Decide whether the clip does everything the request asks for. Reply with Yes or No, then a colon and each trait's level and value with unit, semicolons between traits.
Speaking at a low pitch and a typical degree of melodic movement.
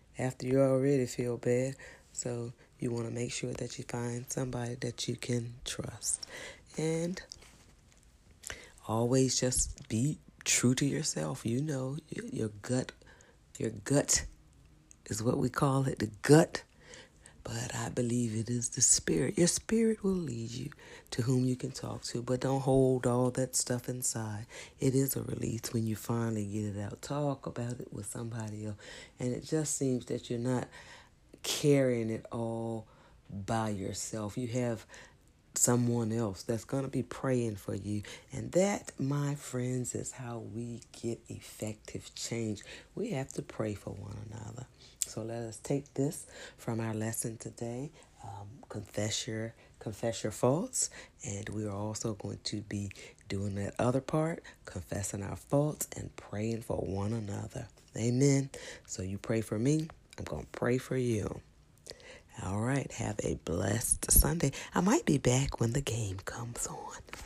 Yes: low, 120 Hz; average, 3.3 semitones